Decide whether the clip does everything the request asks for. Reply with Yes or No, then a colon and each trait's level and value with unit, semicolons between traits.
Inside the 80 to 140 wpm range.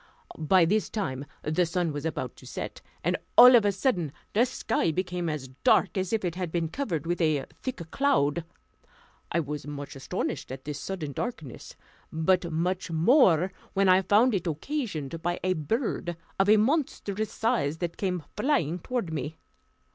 No: average, 170 wpm